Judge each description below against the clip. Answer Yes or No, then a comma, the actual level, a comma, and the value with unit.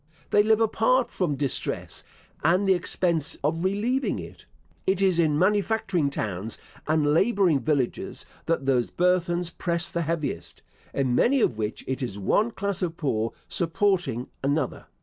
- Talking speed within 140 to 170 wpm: Yes, average, 150 wpm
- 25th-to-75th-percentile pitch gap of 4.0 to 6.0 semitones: Yes, wide, 5.6 semitones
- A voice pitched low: No, medium, 170 Hz